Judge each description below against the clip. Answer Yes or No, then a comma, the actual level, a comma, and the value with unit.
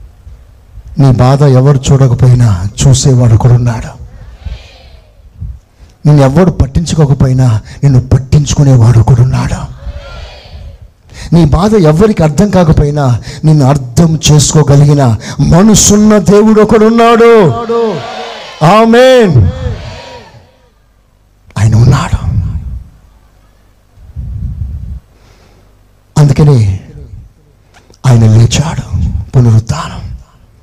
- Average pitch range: No, wide, 7.2 semitones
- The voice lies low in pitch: Yes, low, 125 Hz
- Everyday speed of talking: No, slow, 55 wpm